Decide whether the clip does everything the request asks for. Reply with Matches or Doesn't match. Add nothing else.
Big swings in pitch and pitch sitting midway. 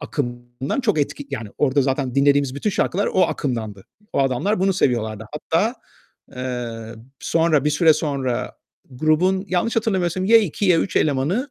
Matches